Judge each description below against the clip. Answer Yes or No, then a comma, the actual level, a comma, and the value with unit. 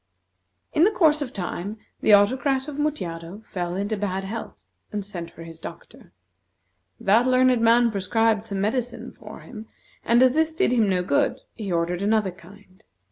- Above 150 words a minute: Yes, average, 170 wpm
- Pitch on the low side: No, high, 215 Hz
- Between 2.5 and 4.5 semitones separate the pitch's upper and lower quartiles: No, average, 4.9 semitones